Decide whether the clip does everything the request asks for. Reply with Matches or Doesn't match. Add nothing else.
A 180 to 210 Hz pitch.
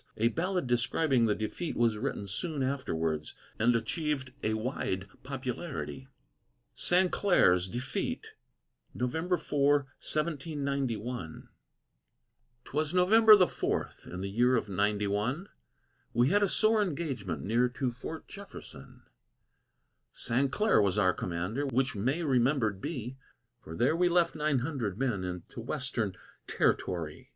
Doesn't match